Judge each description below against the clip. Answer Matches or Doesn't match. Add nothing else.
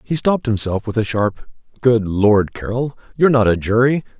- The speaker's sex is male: Matches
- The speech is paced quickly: Doesn't match